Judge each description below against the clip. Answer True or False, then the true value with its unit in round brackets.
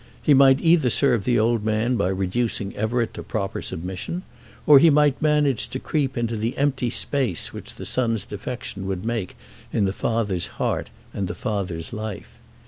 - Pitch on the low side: True (115 Hz)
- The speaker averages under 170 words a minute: False (175 wpm)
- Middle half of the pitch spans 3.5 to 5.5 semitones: True (5.0 semitones)